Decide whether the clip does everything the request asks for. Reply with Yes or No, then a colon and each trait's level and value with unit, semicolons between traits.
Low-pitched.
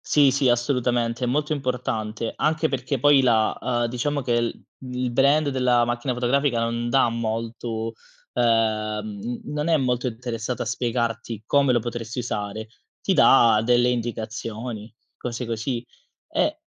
Yes: low, 120 Hz